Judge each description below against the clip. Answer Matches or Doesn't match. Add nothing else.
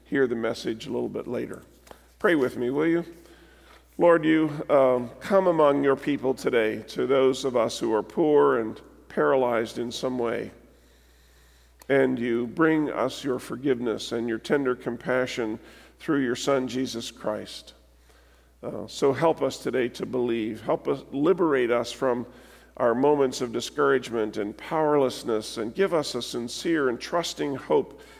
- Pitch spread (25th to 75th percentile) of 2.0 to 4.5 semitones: Matches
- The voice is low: Matches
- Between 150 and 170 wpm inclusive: Matches